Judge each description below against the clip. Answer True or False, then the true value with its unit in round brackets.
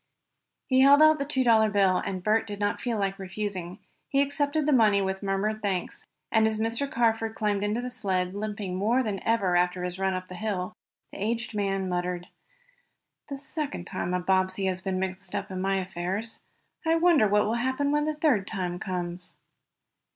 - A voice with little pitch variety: False (3.8 semitones)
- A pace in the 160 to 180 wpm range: False (195 wpm)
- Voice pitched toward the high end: True (205 Hz)